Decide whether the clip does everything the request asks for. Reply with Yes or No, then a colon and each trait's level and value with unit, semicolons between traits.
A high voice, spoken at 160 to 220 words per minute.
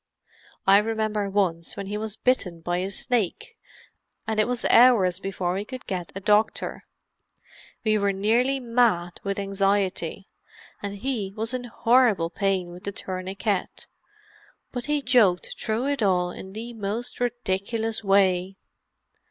No: high, 200 Hz; average, 145 wpm